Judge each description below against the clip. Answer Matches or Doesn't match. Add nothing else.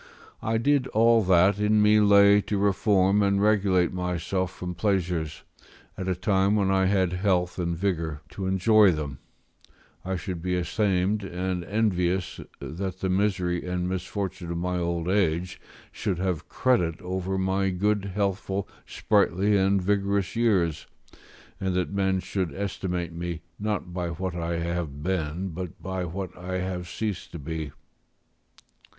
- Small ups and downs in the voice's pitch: Matches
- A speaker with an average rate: Matches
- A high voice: Doesn't match